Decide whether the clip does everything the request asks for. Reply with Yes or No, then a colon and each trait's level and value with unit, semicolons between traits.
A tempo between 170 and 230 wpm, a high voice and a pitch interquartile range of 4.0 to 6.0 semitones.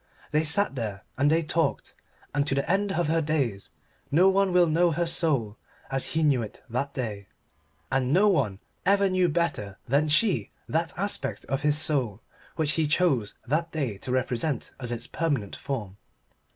No: average, 180 wpm; medium, 150 Hz; average, 5.1 semitones